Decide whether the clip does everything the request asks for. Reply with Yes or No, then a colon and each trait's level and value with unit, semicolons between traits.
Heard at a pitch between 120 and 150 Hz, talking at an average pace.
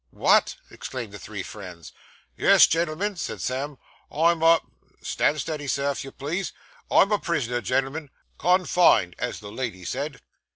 Yes: medium, 140 Hz; average, 155 wpm